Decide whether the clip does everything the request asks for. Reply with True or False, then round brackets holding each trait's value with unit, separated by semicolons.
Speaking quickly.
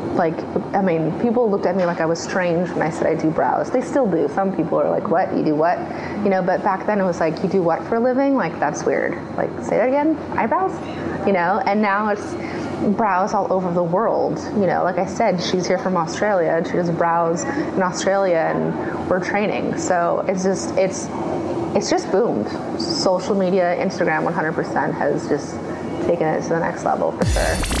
True (215 wpm)